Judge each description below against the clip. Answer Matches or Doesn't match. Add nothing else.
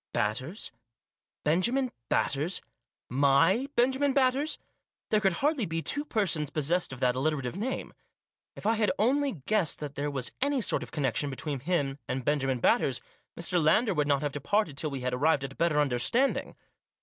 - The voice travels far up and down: Matches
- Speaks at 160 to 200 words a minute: Matches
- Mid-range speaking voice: Matches